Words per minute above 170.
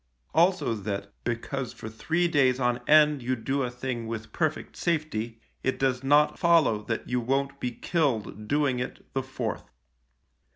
No: average, 160 wpm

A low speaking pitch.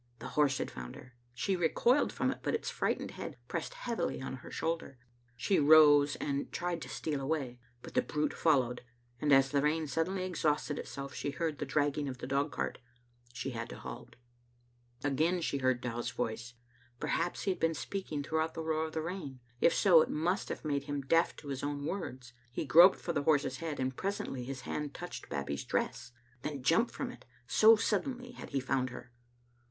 No: medium, 145 Hz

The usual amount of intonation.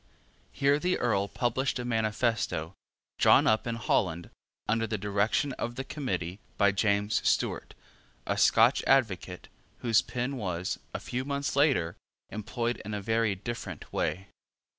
Yes: average, 3.7 semitones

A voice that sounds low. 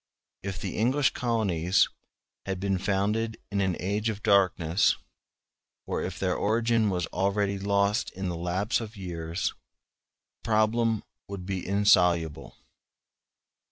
Yes: low, 100 Hz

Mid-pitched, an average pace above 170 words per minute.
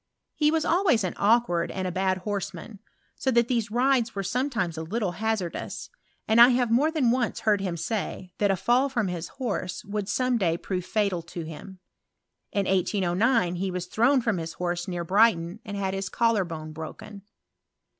No: high, 200 Hz; average, 185 wpm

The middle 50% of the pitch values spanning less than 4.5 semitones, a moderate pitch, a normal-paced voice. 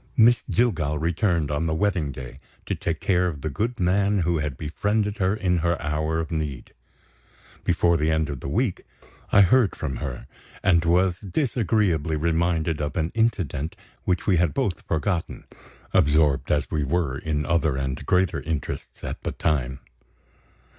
No: average, 3.8 semitones; very low, 80 Hz; average, 165 wpm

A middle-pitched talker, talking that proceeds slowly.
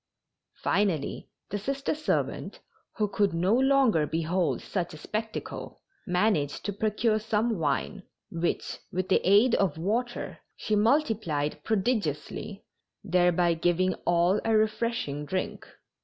No: high, 200 Hz; slow, 120 wpm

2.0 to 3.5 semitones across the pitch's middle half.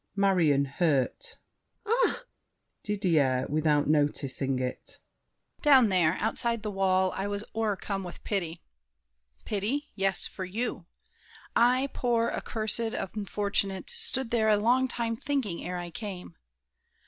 No: average, 5.0 semitones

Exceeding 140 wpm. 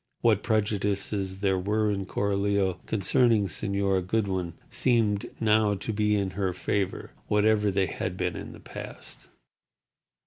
No: slow, 135 wpm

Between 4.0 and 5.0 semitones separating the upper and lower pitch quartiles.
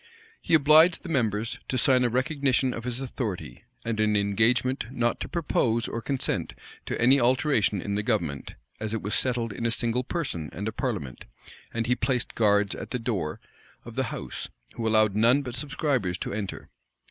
No: average, 3.5 semitones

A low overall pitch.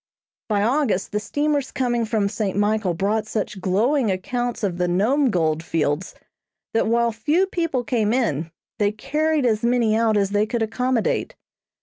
No: high, 220 Hz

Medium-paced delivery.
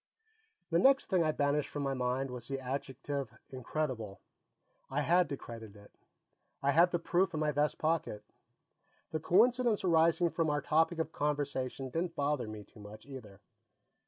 Yes: average, 165 wpm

